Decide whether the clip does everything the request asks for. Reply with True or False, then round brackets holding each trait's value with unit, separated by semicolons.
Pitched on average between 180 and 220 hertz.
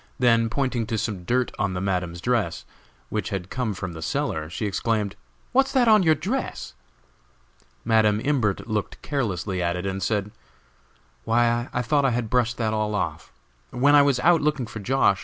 False (115 Hz)